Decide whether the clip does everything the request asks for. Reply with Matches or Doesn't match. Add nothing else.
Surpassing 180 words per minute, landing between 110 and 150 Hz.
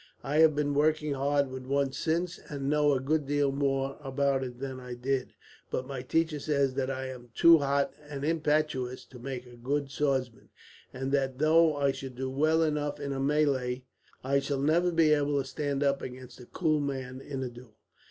Matches